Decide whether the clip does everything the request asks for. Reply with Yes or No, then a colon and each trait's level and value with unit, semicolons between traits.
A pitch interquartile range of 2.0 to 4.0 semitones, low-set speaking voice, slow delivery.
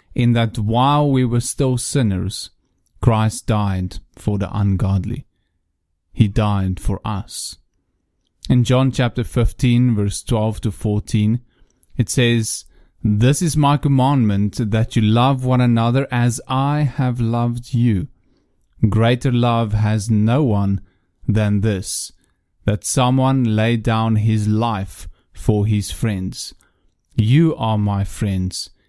Yes: average, 3.6 semitones; low, 110 Hz; slow, 125 wpm